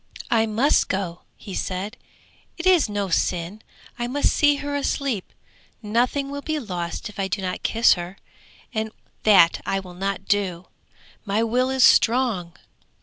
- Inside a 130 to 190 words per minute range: Yes, average, 155 wpm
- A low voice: No, high, 210 Hz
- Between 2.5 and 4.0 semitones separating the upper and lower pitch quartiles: No, average, 5.3 semitones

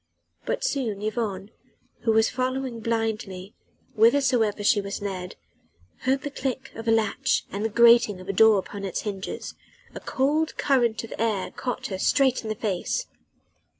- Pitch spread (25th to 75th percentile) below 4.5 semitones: Yes, average, 3.8 semitones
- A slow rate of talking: No, average, 160 wpm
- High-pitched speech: Yes, high, 225 Hz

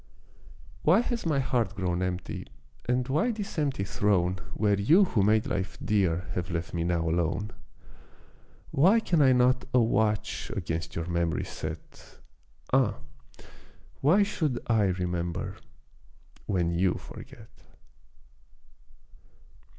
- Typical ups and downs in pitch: No, wide, 7.2 semitones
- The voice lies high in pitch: No, low, 100 Hz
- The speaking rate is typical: No, slow, 120 wpm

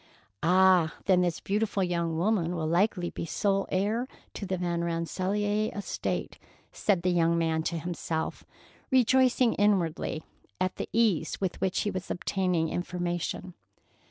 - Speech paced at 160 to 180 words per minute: No, average, 140 wpm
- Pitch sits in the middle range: Yes, medium, 180 Hz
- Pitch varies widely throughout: No, average, 3.1 semitones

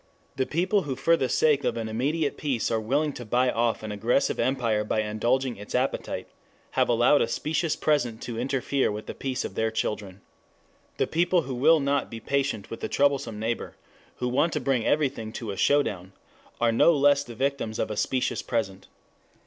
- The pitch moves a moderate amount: Yes, average, 4.1 semitones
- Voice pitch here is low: Yes, low, 125 Hz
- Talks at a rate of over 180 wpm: Yes, average, 195 wpm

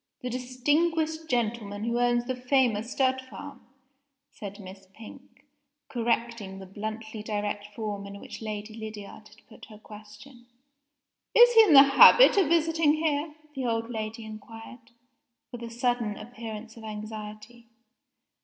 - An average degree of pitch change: Yes, average, 3.5 semitones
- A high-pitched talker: Yes, high, 230 Hz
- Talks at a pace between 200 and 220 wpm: No, average, 140 wpm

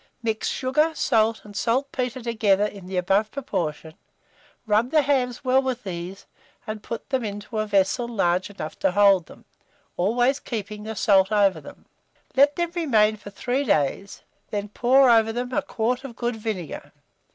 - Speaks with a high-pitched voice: Yes, high, 220 Hz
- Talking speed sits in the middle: Yes, average, 165 wpm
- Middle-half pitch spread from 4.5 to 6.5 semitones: No, average, 3.9 semitones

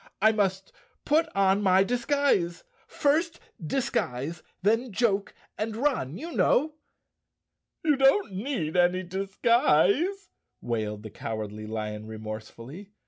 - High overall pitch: Yes, high, 195 Hz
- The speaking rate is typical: No, slow, 105 wpm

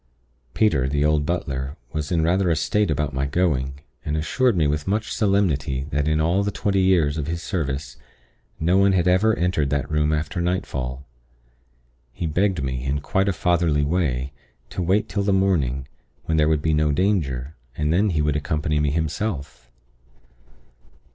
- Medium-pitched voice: No, very low, 80 Hz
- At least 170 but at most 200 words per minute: Yes, average, 175 wpm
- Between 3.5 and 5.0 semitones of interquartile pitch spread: Yes, average, 4.2 semitones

